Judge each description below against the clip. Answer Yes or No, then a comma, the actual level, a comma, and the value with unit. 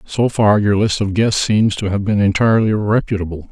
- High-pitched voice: No, low, 105 Hz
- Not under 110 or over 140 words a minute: No, fast, 205 wpm